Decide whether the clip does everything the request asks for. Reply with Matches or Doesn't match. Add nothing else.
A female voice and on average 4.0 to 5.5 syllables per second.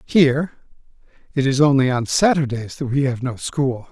Doesn't match